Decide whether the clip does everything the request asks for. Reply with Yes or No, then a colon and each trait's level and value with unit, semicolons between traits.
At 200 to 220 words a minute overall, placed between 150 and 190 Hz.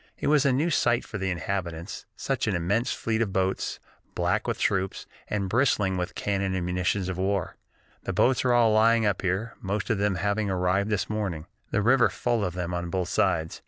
No: fast, 205 wpm; low, 100 Hz